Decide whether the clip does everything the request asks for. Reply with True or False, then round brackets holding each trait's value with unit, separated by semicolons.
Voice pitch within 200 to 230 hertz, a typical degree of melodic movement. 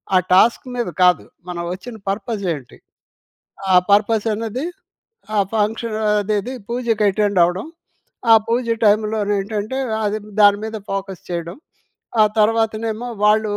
False (210 Hz; 2.2 semitones)